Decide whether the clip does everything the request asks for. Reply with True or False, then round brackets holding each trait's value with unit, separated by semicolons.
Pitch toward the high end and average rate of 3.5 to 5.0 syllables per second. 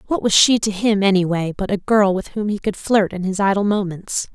False (200 Hz; 5.4 syllables/s)